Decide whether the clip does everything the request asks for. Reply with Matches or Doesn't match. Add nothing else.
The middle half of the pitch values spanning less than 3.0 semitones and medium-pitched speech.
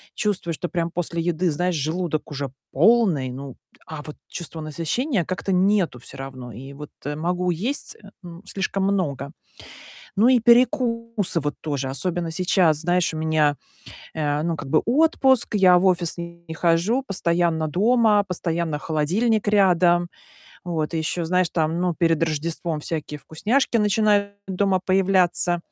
Doesn't match